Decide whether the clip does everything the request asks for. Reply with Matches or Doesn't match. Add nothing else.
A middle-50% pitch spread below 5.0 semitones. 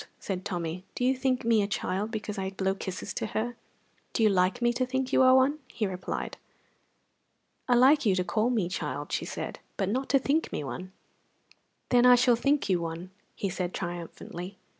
Doesn't match